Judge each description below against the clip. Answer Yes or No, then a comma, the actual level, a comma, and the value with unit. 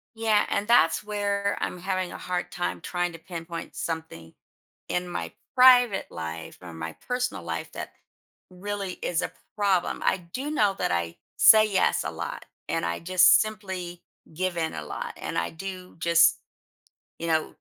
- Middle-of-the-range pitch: Yes, medium, 180 Hz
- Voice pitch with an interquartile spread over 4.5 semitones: No, average, 3.9 semitones